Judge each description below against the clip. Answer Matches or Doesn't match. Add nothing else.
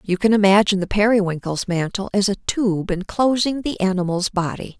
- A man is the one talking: Doesn't match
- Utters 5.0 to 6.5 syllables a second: Matches